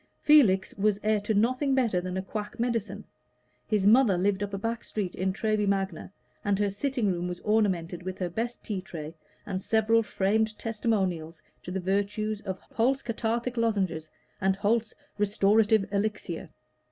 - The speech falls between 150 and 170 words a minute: Yes, average, 165 wpm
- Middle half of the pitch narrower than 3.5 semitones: Yes, average, 2.8 semitones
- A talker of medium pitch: No, high, 205 Hz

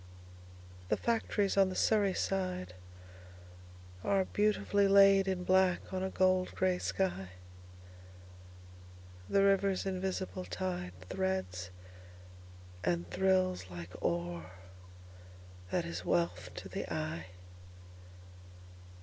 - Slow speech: Yes, slow, 90 wpm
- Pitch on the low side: Yes, very low, 90 Hz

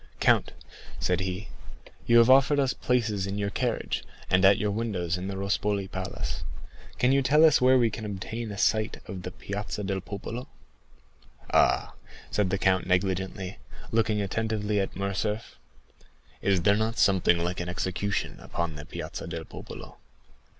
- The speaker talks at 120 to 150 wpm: No, average, 160 wpm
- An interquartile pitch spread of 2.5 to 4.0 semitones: Yes, average, 3.0 semitones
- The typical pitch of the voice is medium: No, low, 100 Hz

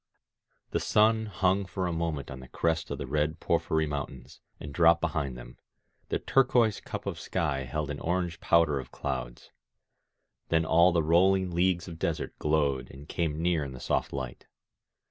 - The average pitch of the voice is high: No, very low, 80 Hz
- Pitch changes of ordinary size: Yes, average, 3.8 semitones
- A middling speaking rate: Yes, average, 175 wpm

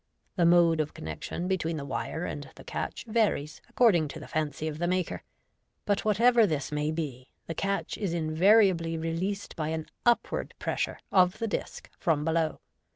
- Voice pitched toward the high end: No, medium, 165 Hz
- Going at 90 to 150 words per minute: No, average, 175 wpm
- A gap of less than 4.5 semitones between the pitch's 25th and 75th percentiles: Yes, average, 3.9 semitones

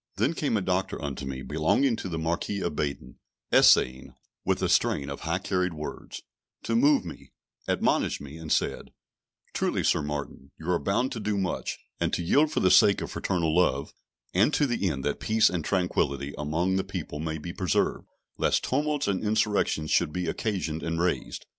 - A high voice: No, very low, 90 Hz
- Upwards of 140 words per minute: Yes, average, 190 wpm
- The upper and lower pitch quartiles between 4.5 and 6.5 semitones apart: Yes, average, 4.9 semitones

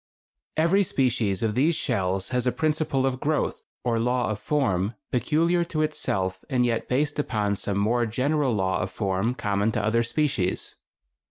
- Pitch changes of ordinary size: No, wide, 6.2 semitones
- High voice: No, low, 125 Hz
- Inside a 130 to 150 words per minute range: No, average, 165 wpm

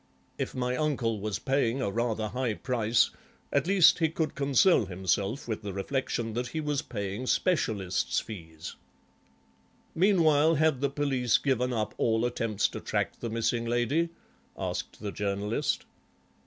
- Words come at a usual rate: Yes, average, 145 wpm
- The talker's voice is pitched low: Yes, low, 120 Hz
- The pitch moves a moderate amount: Yes, average, 4.7 semitones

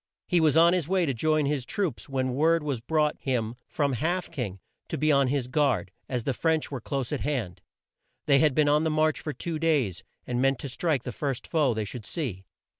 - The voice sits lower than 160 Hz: Yes, medium, 140 Hz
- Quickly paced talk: Yes, fast, 225 wpm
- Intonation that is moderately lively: Yes, average, 3.9 semitones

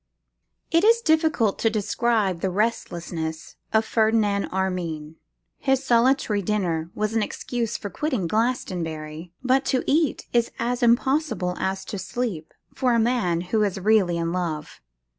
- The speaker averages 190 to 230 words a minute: No, average, 145 wpm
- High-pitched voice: Yes, high, 215 Hz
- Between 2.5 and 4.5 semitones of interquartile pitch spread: No, average, 5.3 semitones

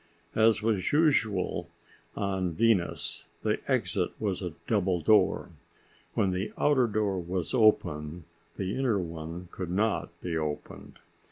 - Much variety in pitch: No, average, 3.9 semitones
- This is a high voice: No, very low, 95 Hz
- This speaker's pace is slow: Yes, slow, 125 wpm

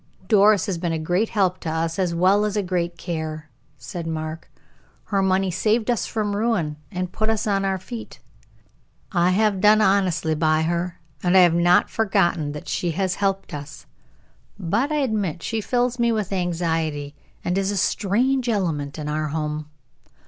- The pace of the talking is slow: No, average, 175 wpm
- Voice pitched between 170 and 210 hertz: Yes, medium, 185 Hz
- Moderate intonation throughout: Yes, average, 4.1 semitones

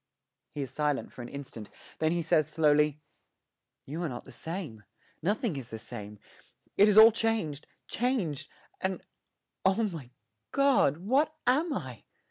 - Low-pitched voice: No, medium, 155 Hz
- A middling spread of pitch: No, wide, 7.5 semitones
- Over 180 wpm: No, average, 150 wpm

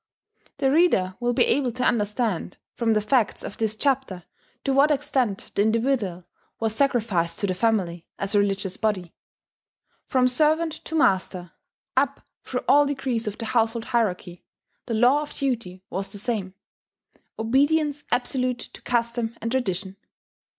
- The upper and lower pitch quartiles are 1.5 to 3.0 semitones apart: No, average, 5.0 semitones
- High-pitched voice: Yes, high, 230 Hz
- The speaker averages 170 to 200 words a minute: No, average, 150 wpm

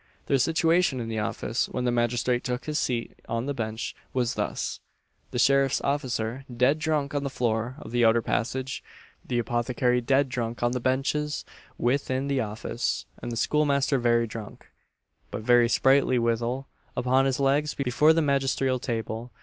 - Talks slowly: No, average, 165 wpm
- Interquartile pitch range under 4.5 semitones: Yes, average, 2.7 semitones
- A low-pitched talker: Yes, low, 125 Hz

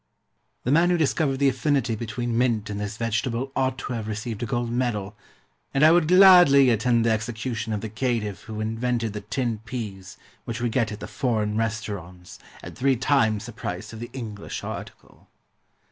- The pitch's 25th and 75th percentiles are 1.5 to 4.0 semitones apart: Yes, average, 3.2 semitones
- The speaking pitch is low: Yes, low, 115 Hz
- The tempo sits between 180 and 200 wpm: Yes, average, 185 wpm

